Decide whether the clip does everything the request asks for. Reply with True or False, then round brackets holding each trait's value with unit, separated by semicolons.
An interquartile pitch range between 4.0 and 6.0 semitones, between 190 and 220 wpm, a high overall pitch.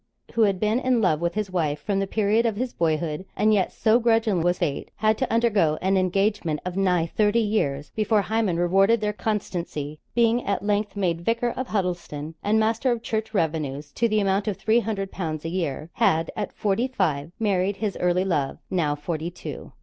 True (4.4 semitones; 200 wpm; 195 Hz)